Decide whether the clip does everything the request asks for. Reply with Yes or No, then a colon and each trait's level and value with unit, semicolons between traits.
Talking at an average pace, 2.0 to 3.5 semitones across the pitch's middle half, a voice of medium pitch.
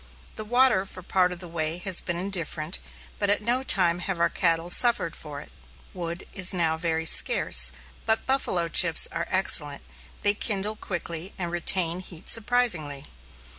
Yes: average, 165 wpm; average, 3.2 semitones; medium, 175 Hz